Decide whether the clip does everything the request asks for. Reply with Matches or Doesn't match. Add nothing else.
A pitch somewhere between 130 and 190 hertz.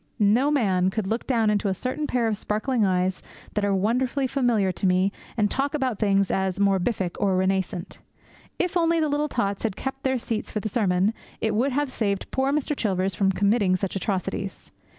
Doesn't match